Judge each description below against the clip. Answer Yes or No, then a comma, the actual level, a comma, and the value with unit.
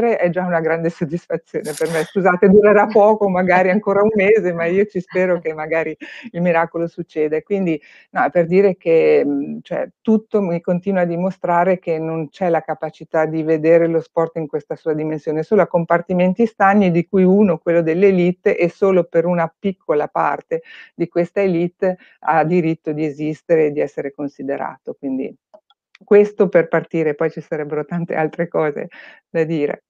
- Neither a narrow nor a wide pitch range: Yes, average, 3.4 semitones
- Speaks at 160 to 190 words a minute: Yes, fast, 170 wpm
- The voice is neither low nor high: Yes, medium, 175 Hz